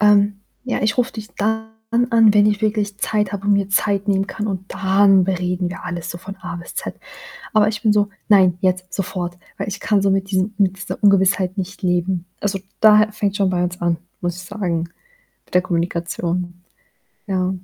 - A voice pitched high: Yes, high, 195 Hz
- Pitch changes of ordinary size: No, narrow, 2.3 semitones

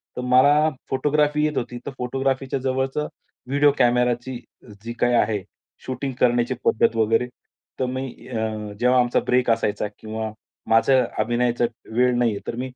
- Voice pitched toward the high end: No, low, 125 Hz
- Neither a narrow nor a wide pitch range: No, narrow, 2.1 semitones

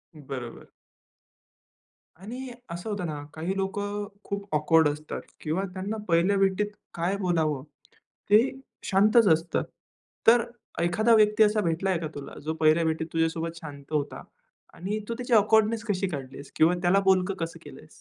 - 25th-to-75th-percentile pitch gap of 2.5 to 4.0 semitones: No, average, 4.4 semitones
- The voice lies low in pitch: No, medium, 180 Hz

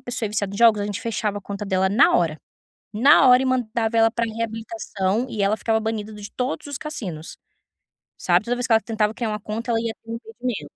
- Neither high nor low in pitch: No, high, 225 Hz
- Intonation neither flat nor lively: No, narrow, 2.2 semitones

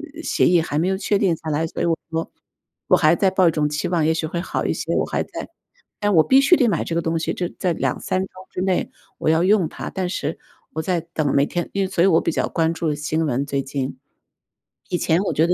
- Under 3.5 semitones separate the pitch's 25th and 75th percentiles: Yes, average, 3.0 semitones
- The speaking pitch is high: No, medium, 165 Hz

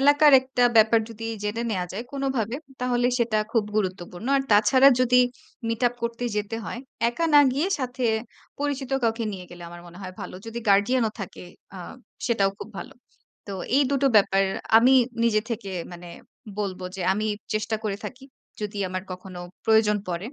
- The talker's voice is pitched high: Yes, high, 225 Hz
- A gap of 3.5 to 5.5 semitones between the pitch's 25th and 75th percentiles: Yes, average, 4.1 semitones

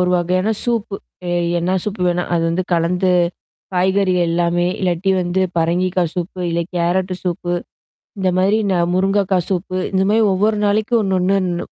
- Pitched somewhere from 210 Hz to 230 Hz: No, medium, 185 Hz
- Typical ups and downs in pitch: No, narrow, 1.8 semitones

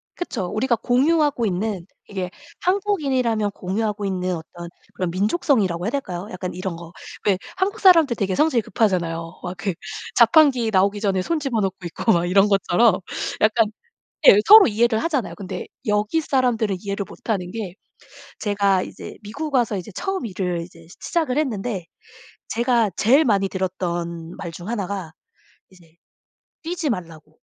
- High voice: Yes, high, 205 Hz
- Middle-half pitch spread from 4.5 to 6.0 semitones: Yes, average, 5.3 semitones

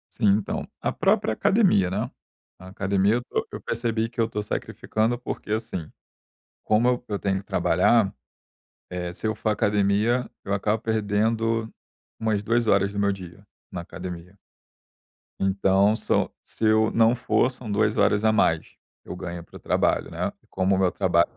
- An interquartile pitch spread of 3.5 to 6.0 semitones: No, narrow, 2.6 semitones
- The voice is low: Yes, low, 105 Hz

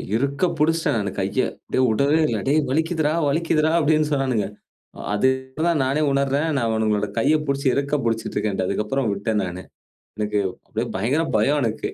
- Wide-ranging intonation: Yes, wide, 6.0 semitones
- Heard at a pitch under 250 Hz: Yes, low, 135 Hz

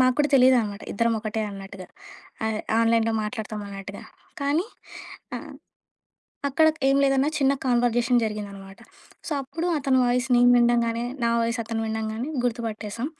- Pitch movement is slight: No, average, 3.0 semitones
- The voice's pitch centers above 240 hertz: No, high, 230 Hz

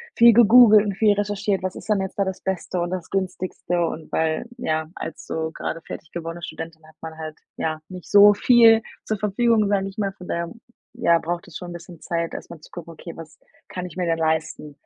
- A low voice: No, medium, 180 Hz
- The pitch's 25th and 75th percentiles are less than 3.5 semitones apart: No, average, 3.9 semitones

